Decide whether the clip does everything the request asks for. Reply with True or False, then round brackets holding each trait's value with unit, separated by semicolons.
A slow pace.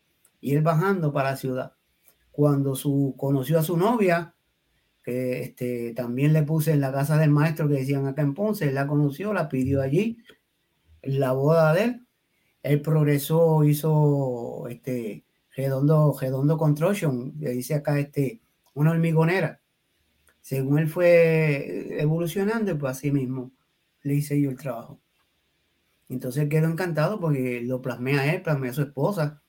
False (150 wpm)